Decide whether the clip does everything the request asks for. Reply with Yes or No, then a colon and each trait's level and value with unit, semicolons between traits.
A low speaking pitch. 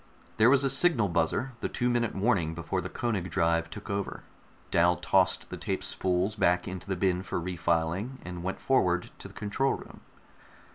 Yes: very low, 95 Hz